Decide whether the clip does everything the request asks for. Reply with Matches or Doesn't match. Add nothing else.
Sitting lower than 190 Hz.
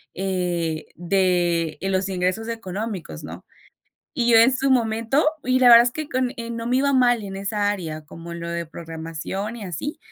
Doesn't match